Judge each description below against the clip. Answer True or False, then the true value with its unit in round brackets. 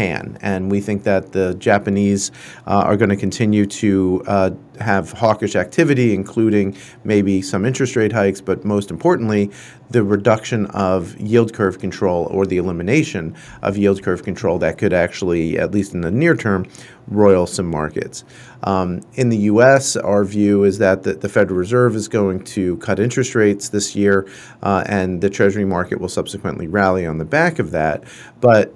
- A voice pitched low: True (100 Hz)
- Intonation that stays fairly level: True (2.3 semitones)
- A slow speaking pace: False (175 wpm)